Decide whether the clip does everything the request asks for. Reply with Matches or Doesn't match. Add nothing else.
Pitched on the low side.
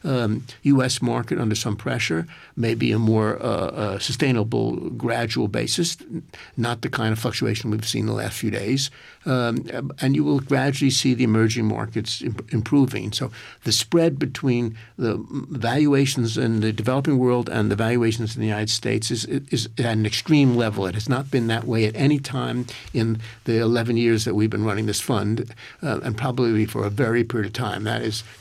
Matches